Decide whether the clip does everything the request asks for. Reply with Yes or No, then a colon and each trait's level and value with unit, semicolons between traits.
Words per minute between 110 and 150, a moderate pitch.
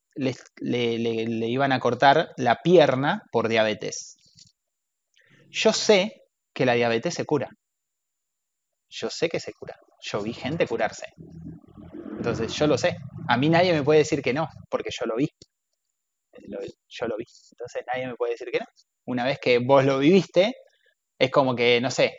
No: average, 170 wpm; medium, 145 Hz